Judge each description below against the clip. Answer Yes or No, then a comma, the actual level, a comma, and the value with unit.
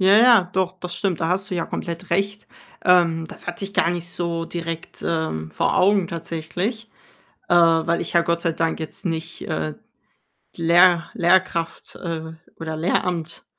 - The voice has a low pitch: No, medium, 170 Hz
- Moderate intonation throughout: No, narrow, 2.0 semitones